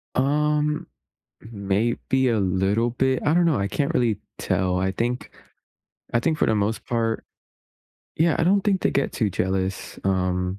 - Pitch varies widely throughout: Yes, wide, 6.9 semitones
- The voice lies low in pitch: Yes, low, 115 Hz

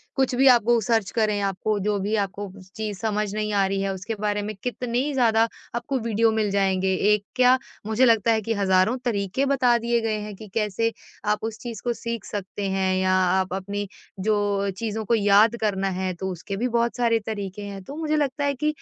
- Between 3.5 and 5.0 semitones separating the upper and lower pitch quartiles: No, average, 2.8 semitones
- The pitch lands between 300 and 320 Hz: No, high, 215 Hz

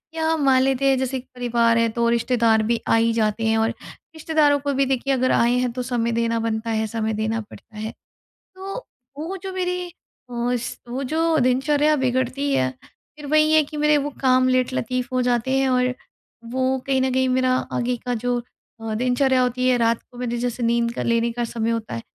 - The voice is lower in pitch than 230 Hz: No, very high, 250 Hz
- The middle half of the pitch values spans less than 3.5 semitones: Yes, average, 2.8 semitones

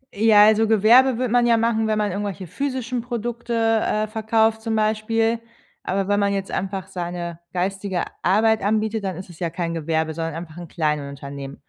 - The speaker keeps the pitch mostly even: No, average, 4.1 semitones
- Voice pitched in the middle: No, high, 205 Hz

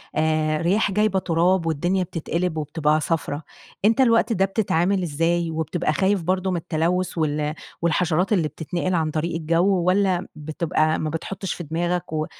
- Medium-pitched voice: Yes, medium, 170 Hz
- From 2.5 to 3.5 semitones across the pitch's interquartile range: Yes, average, 2.8 semitones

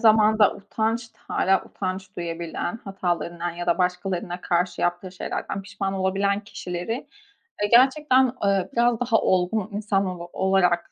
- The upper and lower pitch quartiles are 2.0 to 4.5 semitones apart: Yes, average, 3.3 semitones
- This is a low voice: No, high, 195 Hz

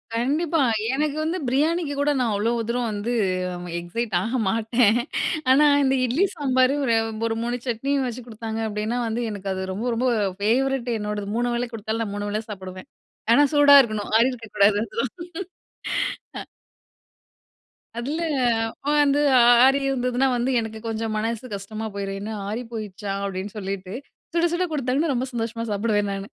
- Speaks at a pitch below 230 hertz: No, high, 235 Hz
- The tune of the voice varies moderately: Yes, average, 4.0 semitones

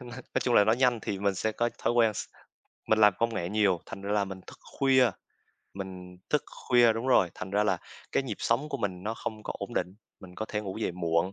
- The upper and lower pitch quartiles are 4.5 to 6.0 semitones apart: No, average, 3.8 semitones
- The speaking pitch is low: Yes, low, 105 Hz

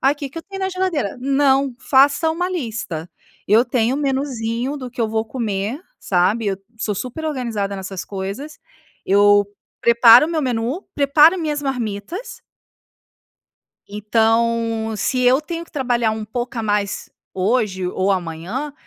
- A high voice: Yes, high, 240 Hz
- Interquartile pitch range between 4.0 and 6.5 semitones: Yes, average, 5.1 semitones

